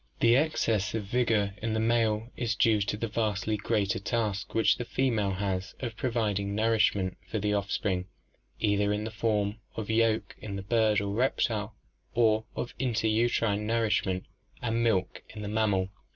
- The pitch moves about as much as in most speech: No, narrow, 2.1 semitones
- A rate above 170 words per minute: No, average, 165 wpm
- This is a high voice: No, low, 110 Hz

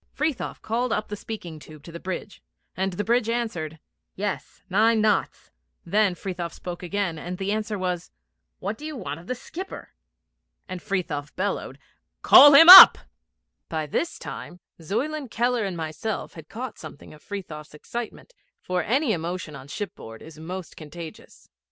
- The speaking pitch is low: No, high, 190 Hz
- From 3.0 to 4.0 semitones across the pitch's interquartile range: No, average, 5.2 semitones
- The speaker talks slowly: No, average, 160 wpm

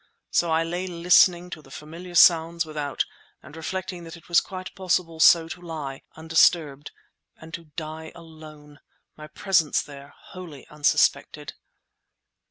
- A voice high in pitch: No, medium, 165 Hz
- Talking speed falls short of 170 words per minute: Yes, average, 140 wpm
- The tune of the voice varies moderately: No, narrow, 2.2 semitones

